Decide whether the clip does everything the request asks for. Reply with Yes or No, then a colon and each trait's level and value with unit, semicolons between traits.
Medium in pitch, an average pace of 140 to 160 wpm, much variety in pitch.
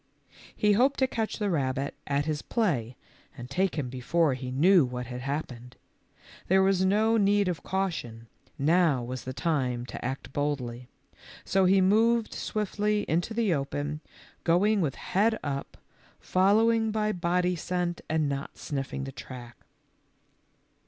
Yes: medium, 165 Hz; average, 145 wpm; wide, 6.9 semitones